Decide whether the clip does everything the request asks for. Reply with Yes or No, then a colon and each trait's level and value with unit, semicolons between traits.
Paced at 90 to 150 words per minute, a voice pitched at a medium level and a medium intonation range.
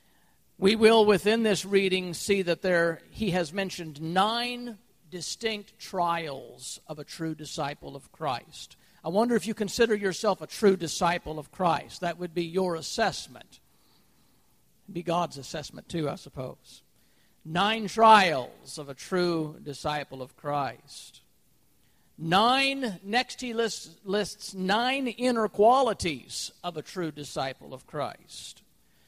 Yes: slow, 135 wpm; medium, 180 Hz; average, 4.8 semitones